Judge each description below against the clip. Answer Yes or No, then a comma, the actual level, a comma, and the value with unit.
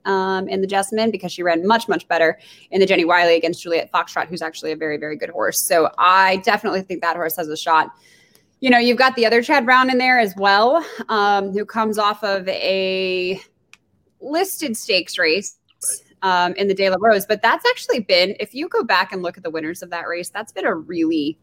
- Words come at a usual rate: No, fast, 225 wpm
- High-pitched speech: Yes, high, 195 Hz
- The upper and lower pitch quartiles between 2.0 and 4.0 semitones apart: No, average, 4.7 semitones